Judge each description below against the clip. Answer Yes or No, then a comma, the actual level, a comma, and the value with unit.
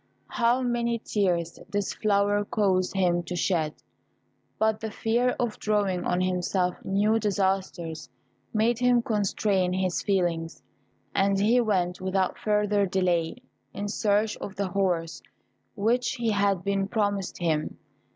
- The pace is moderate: No, slow, 130 wpm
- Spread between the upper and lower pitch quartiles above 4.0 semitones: No, average, 2.8 semitones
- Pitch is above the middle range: Yes, high, 200 Hz